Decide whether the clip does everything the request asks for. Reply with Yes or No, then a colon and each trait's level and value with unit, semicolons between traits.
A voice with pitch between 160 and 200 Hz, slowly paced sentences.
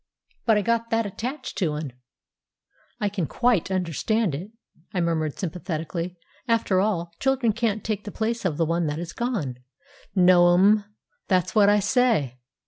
No: high, 190 Hz; average, 160 wpm